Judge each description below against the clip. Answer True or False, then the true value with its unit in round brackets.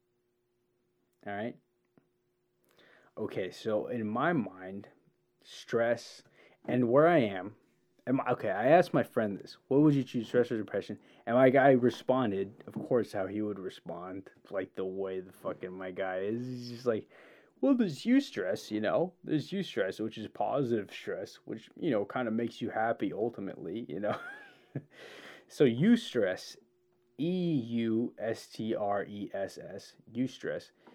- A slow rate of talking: False (165 wpm)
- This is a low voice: True (120 Hz)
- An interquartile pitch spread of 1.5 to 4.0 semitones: False (5.3 semitones)